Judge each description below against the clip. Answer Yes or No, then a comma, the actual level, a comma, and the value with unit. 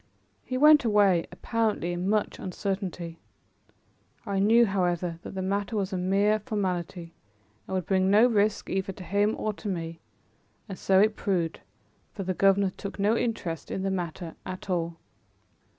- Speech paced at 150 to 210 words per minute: Yes, average, 165 wpm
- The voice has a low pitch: No, high, 195 Hz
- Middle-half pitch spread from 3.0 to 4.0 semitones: No, narrow, 2.6 semitones